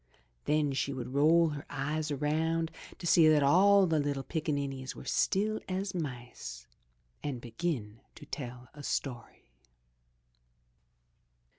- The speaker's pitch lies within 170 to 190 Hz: No, medium, 145 Hz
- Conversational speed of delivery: No, slow, 125 wpm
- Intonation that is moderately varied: Yes, average, 3.5 semitones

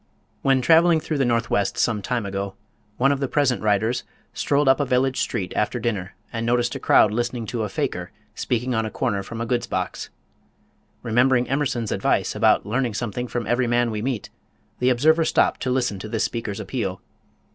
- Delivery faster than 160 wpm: Yes, average, 190 wpm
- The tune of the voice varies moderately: Yes, average, 3.0 semitones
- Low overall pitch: Yes, low, 120 Hz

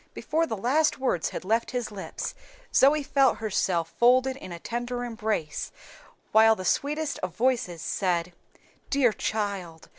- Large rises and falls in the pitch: Yes, wide, 5.8 semitones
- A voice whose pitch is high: Yes, high, 225 Hz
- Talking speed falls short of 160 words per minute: Yes, average, 145 wpm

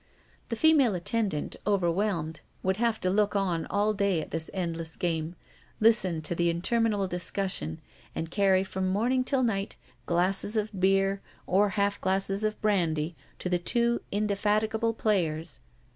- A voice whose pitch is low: No, high, 195 Hz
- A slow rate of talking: No, average, 145 wpm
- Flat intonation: No, average, 3.6 semitones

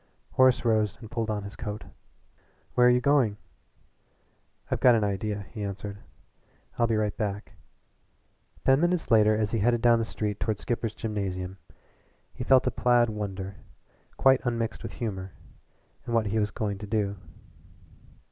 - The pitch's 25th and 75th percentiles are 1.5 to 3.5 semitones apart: Yes, narrow, 2.6 semitones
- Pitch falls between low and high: No, low, 110 Hz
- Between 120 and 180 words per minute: Yes, average, 160 wpm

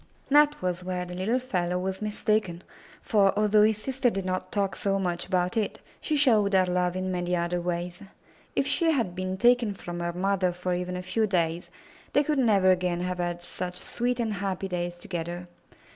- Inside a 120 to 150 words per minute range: No, average, 195 wpm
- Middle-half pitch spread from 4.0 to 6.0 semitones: No, average, 3.1 semitones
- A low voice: No, medium, 185 Hz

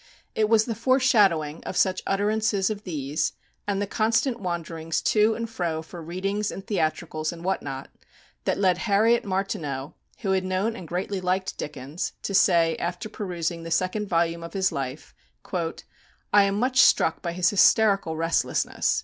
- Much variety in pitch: No, average, 3.8 semitones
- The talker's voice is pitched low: No, medium, 185 Hz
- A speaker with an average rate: Yes, average, 165 wpm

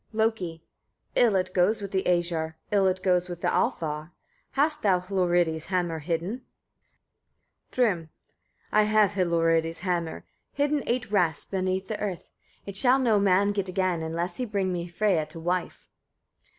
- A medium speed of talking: Yes, average, 160 wpm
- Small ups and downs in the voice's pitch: No, average, 3.3 semitones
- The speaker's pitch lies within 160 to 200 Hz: Yes, medium, 185 Hz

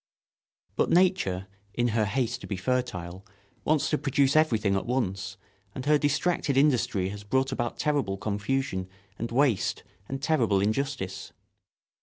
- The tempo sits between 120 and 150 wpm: Yes, average, 140 wpm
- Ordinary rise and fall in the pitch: No, wide, 5.9 semitones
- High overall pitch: No, low, 120 Hz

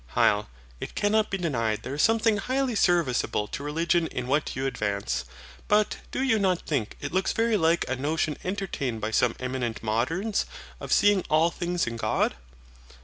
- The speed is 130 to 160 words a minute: No, average, 175 wpm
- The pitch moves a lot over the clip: Yes, wide, 7.9 semitones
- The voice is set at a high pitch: No, medium, 160 Hz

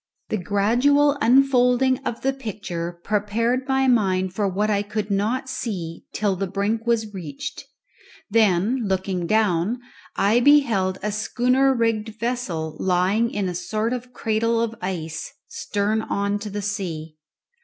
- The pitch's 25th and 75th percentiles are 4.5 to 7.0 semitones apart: No, average, 4.0 semitones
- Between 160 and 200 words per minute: No, average, 145 wpm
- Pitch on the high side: Yes, high, 210 Hz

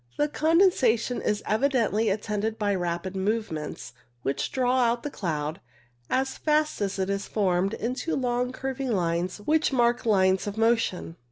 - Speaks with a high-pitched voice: Yes, high, 220 Hz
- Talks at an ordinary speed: Yes, average, 155 wpm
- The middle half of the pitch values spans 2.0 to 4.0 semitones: No, average, 5.2 semitones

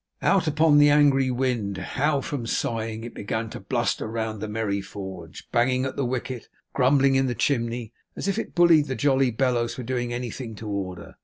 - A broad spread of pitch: No, average, 3.5 semitones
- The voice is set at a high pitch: No, low, 125 Hz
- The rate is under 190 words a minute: No, average, 200 wpm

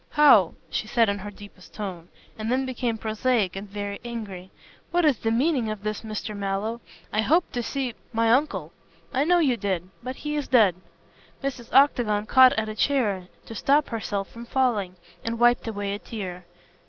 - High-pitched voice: Yes, high, 225 Hz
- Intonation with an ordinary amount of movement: Yes, average, 4.1 semitones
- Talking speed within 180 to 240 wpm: Yes, average, 190 wpm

